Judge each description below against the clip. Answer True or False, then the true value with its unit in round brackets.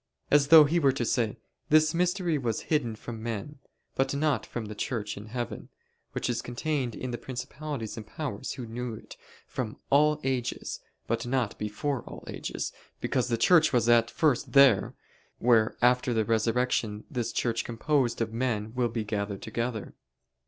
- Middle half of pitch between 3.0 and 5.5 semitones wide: True (3.7 semitones)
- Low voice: True (120 Hz)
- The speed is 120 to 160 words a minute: False (170 wpm)